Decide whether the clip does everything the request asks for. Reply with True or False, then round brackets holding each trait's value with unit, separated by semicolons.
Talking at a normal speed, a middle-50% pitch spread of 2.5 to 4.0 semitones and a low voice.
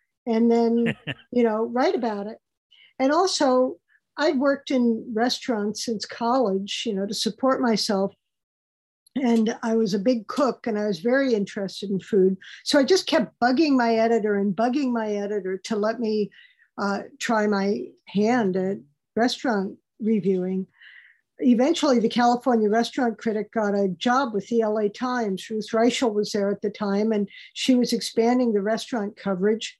False (160 wpm; 3.1 semitones; 225 Hz)